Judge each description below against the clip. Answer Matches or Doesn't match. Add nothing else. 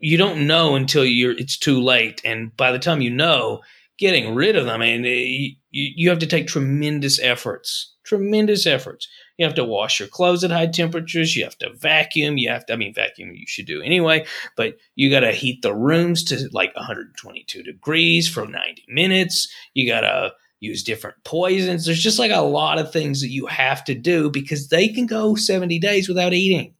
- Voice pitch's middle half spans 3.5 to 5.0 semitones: Matches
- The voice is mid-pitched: Matches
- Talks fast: Matches